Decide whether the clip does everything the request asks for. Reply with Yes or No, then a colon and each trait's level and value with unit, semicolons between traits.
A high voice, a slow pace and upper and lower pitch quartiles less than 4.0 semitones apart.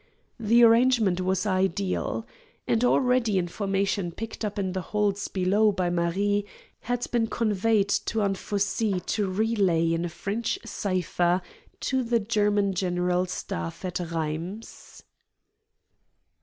Yes: high, 200 Hz; slow, 120 wpm; average, 3.3 semitones